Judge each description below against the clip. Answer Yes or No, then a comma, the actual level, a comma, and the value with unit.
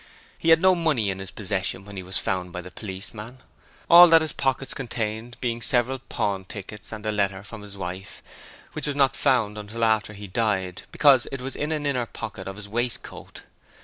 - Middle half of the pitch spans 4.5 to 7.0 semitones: Yes, average, 5.2 semitones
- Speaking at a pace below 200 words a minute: No, fast, 205 wpm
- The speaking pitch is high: No, low, 110 Hz